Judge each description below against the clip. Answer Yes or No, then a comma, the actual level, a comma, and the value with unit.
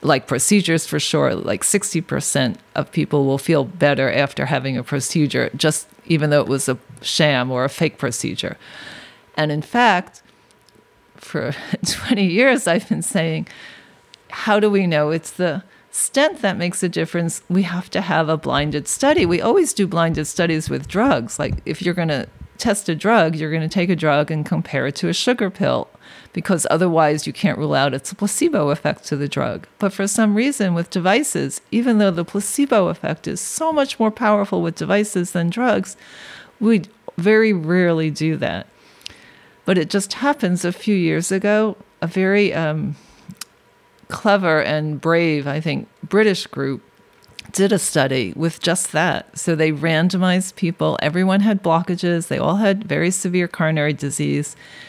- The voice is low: No, medium, 175 Hz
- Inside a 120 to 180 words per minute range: Yes, average, 170 wpm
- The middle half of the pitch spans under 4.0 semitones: No, average, 4.6 semitones